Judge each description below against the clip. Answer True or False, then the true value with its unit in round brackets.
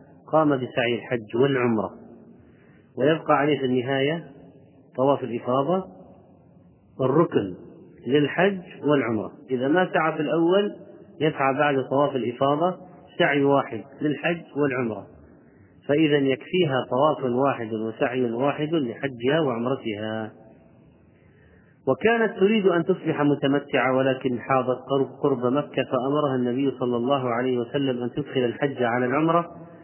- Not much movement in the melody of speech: False (3.4 semitones)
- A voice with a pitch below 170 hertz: True (140 Hz)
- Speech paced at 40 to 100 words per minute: False (110 wpm)